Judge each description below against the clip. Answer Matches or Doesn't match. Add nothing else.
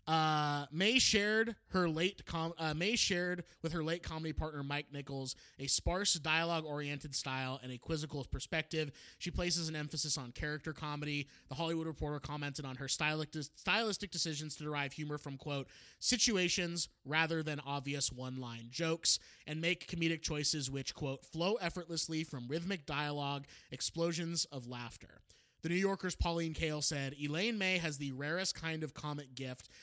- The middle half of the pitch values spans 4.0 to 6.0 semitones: Doesn't match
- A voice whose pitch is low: Doesn't match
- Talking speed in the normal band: Matches